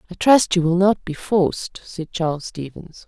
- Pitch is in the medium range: Yes, medium, 175 Hz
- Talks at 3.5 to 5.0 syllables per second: Yes, 4.6 syllables/s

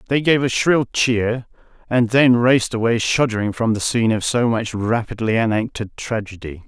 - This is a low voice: Yes, low, 115 Hz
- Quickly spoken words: No, average, 170 wpm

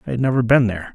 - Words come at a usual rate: No, fast, 320 wpm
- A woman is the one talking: No, male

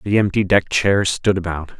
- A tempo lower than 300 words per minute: Yes, average, 200 wpm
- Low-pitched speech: Yes, very low, 95 Hz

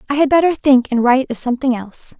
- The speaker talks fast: Yes, fast, 245 wpm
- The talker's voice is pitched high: Yes, very high, 260 Hz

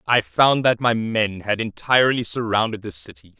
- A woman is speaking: No, male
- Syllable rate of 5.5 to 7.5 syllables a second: No, 5.0 syllables/s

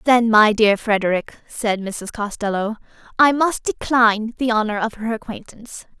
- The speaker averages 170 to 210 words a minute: No, average, 150 wpm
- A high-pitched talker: Yes, high, 220 Hz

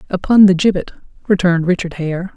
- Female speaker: Yes, female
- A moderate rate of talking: Yes, average, 155 wpm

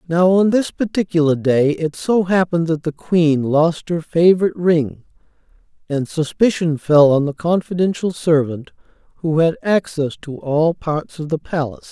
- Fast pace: No, average, 155 wpm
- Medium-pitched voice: Yes, medium, 165 Hz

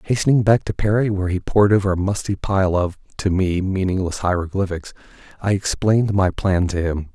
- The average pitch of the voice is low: Yes, very low, 95 Hz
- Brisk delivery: No, average, 185 wpm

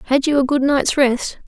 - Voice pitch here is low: No, very high, 270 Hz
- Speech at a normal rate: No, fast, 245 wpm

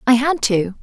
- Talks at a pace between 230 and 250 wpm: No, fast, 215 wpm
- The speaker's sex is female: Yes, female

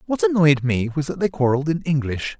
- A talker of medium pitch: Yes, medium, 150 Hz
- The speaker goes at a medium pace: No, fast, 225 wpm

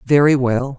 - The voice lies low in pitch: Yes, low, 130 Hz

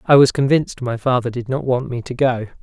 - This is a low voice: Yes, low, 125 Hz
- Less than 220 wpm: No, fast, 250 wpm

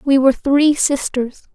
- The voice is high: Yes, very high, 275 Hz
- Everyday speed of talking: Yes, average, 155 wpm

